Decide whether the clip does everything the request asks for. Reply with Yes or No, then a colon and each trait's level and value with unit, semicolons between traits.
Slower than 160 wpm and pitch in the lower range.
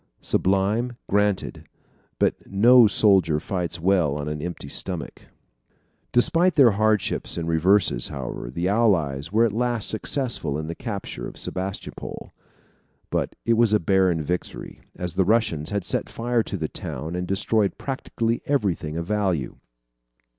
Yes: average, 145 wpm; very low, 95 Hz